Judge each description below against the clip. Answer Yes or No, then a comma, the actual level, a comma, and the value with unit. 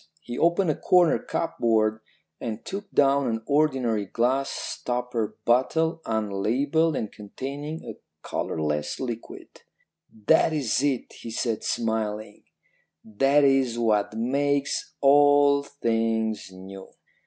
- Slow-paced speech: Yes, slow, 110 wpm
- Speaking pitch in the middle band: No, low, 125 Hz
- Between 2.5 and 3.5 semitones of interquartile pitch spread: No, average, 4.5 semitones